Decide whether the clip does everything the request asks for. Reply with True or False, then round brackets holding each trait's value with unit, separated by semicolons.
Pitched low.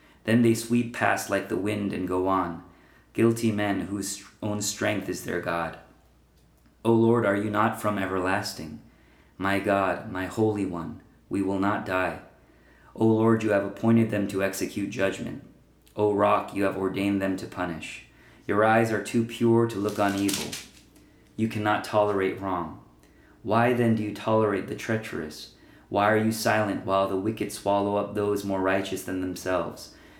True (100 Hz)